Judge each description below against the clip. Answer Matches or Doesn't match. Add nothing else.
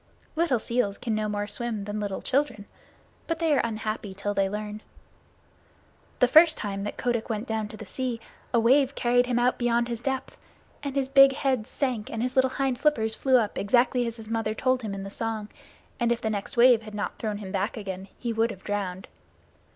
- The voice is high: Matches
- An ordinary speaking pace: Doesn't match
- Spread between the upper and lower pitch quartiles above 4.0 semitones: Doesn't match